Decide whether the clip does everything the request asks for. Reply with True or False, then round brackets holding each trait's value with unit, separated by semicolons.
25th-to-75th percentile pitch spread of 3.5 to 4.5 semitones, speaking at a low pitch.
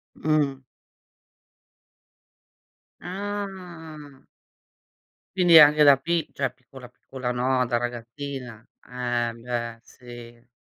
True (4.1 semitones; 130 Hz)